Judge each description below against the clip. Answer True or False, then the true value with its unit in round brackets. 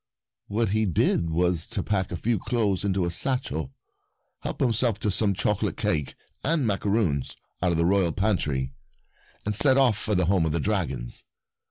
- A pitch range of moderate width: True (4.5 semitones)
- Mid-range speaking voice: False (100 Hz)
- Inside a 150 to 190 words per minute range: True (175 wpm)